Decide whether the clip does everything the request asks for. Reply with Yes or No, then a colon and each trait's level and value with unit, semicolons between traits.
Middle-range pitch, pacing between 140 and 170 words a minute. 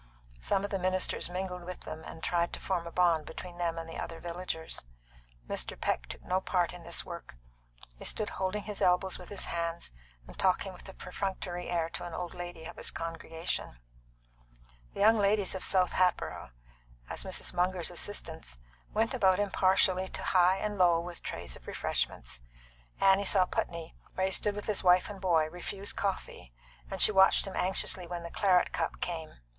No: medium, 180 Hz; average, 185 wpm